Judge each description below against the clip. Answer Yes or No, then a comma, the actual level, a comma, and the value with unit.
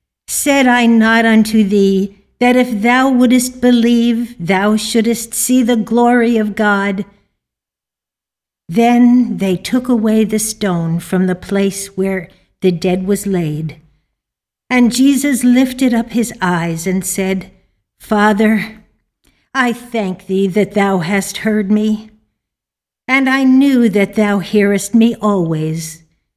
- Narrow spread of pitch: No, average, 3.8 semitones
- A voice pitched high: Yes, high, 215 Hz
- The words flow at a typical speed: No, slow, 125 wpm